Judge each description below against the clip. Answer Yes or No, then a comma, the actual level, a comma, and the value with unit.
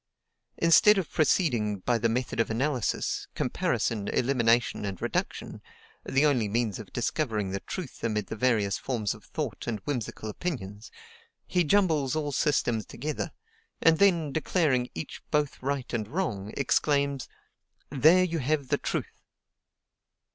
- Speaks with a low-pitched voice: Yes, low, 130 Hz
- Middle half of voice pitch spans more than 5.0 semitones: Yes, wide, 5.6 semitones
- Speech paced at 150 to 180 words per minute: No, average, 140 wpm